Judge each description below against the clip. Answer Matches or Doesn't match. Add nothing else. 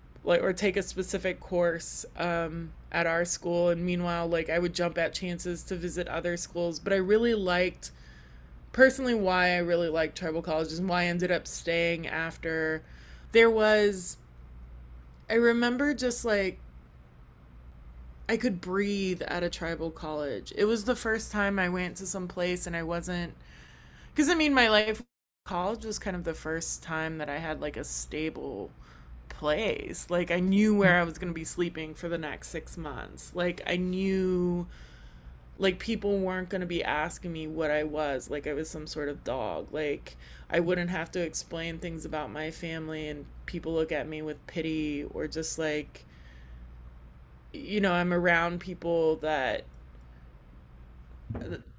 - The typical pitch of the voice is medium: Matches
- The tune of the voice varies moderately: Matches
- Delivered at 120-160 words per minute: Doesn't match